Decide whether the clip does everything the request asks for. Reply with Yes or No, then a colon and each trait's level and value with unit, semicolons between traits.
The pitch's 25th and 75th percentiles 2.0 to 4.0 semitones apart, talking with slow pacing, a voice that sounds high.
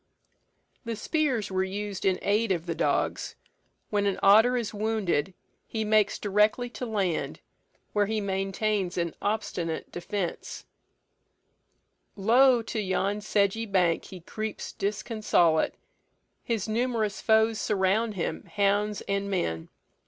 Yes: narrow, 2.5 semitones; slow, 125 wpm; high, 205 Hz